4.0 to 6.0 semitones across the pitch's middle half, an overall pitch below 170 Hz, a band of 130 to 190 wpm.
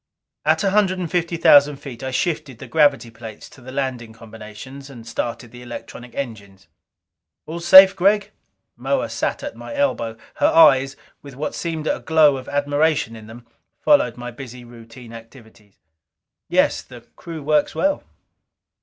Yes: wide, 5.6 semitones; low, 135 Hz; average, 160 wpm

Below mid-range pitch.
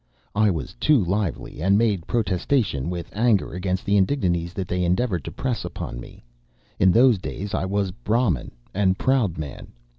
Yes: very low, 95 Hz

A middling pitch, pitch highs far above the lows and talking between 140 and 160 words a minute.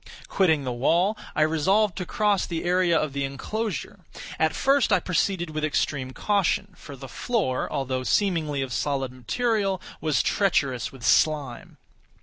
Yes: medium, 160 Hz; wide, 6.3 semitones; average, 150 wpm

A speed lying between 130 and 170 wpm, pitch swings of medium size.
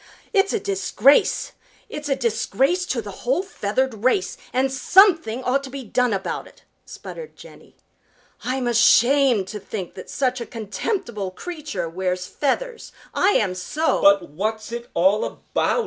No: average, 150 wpm; wide, 6.8 semitones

